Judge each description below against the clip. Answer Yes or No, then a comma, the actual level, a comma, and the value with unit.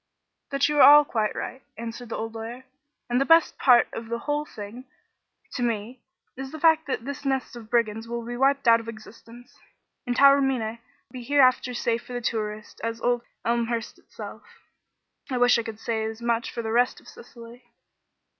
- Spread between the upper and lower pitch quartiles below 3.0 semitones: Yes, narrow, 2.6 semitones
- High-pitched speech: Yes, high, 240 Hz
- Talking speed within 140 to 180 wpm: No, average, 190 wpm